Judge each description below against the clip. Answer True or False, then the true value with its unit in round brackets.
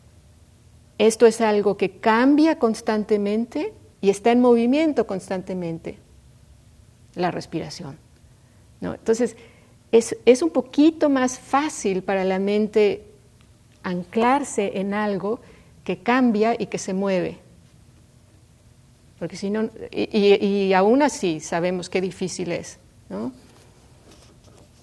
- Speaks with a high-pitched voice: True (195 Hz)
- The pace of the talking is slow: True (110 wpm)